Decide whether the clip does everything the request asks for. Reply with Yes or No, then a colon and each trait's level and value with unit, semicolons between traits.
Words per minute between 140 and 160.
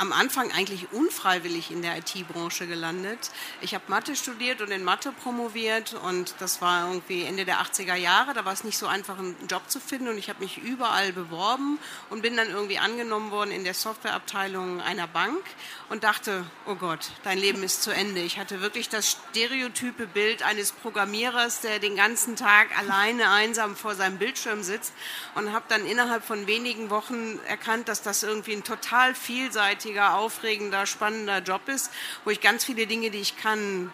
No: average, 185 wpm